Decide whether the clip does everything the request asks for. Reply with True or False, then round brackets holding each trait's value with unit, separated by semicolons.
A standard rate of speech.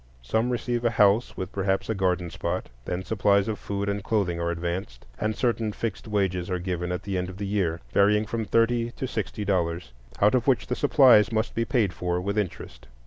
False (210 wpm)